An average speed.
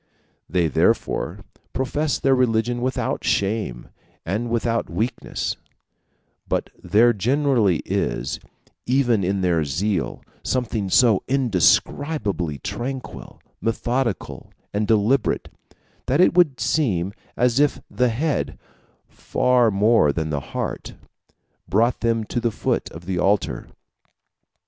No: slow, 110 wpm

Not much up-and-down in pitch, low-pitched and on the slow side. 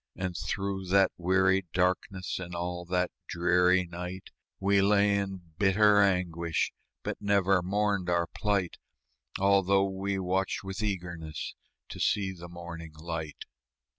Yes: narrow, 1.9 semitones; very low, 95 Hz; slow, 130 wpm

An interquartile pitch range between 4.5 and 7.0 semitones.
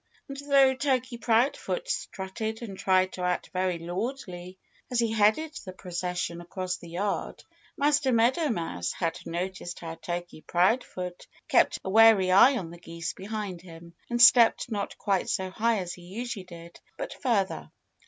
Yes: average, 5.1 semitones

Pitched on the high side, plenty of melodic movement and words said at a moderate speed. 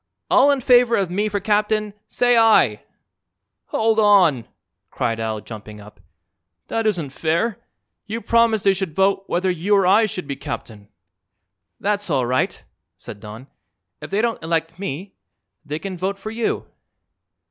Yes: high, 195 Hz; wide, 6.5 semitones; average, 155 wpm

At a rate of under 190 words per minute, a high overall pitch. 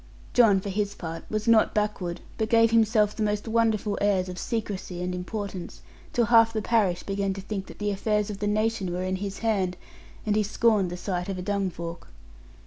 No: fast, 205 wpm; high, 205 Hz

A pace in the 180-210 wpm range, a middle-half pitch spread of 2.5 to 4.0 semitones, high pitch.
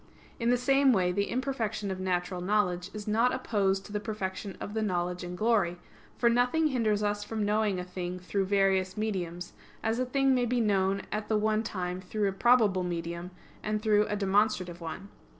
Yes: average, 195 wpm; average, 3.1 semitones; high, 205 Hz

